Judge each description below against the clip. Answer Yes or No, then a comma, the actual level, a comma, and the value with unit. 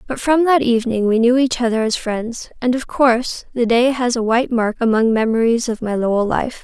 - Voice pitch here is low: No, high, 235 Hz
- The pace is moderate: No, fast, 225 wpm